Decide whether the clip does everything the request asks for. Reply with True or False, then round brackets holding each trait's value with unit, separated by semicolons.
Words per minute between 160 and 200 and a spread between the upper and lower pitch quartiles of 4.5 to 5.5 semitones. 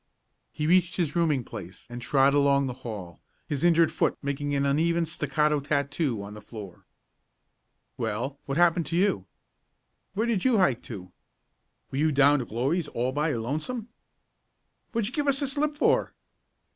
True (170 wpm; 5.0 semitones)